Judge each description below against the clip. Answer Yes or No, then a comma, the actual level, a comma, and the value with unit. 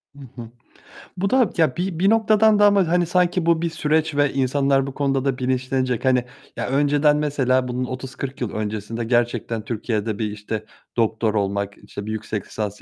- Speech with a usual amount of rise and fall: No, wide, 5.9 semitones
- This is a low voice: Yes, low, 130 Hz